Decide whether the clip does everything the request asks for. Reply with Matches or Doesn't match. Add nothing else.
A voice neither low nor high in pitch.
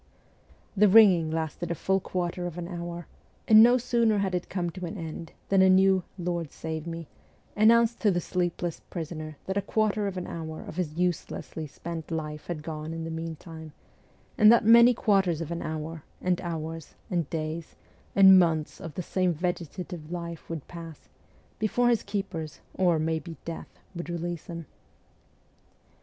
Matches